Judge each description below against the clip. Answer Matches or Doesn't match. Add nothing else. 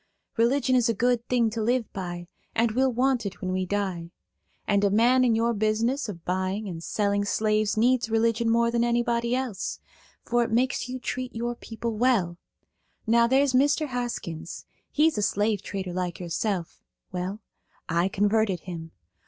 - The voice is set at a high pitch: Matches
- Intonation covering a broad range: Doesn't match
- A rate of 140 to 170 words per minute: Matches